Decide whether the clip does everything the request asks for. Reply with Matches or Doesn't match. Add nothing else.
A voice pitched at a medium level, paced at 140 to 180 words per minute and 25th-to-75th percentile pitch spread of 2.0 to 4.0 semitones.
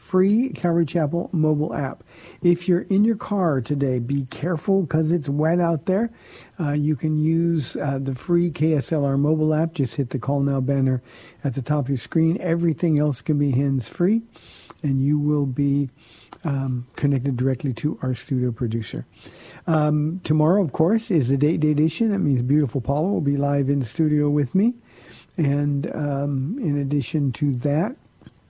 Matches